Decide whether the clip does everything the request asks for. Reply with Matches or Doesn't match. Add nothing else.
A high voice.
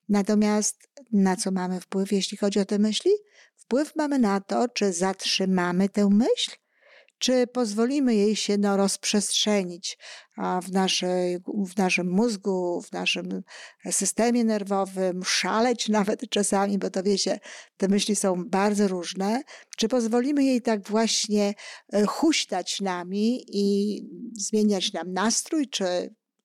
Matches